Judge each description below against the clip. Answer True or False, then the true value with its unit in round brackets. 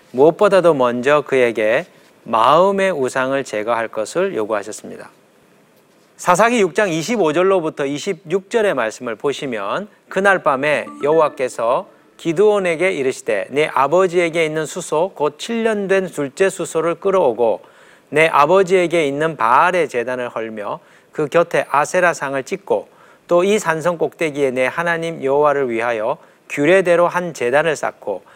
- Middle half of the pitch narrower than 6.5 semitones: True (5.5 semitones)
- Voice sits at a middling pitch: True (165 Hz)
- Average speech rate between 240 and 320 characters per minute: True (295 characters per minute)